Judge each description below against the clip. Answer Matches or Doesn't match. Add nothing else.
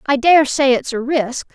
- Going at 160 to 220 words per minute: Doesn't match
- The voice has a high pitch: Matches